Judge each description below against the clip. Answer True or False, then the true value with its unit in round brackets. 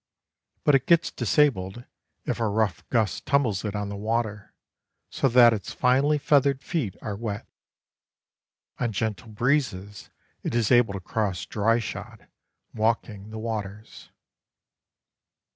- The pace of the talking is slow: True (130 wpm)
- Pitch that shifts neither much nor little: True (3.4 semitones)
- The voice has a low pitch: True (110 Hz)